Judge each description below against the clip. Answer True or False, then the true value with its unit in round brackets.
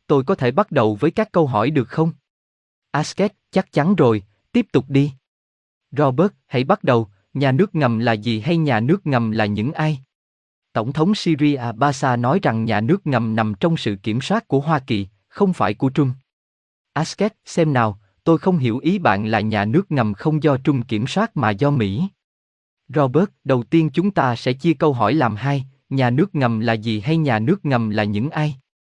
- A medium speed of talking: True (205 wpm)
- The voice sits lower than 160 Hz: True (135 Hz)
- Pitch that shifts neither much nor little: False (6.2 semitones)